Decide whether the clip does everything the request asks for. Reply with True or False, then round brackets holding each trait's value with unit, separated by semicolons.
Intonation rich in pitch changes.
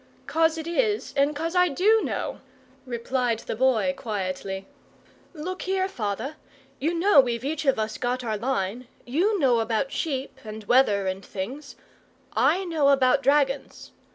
True (6.2 semitones)